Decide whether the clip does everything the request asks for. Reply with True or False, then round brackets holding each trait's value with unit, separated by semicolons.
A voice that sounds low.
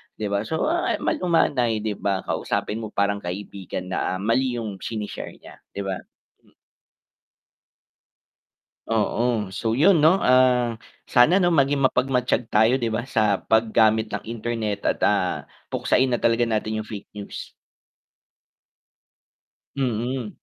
True (115 Hz)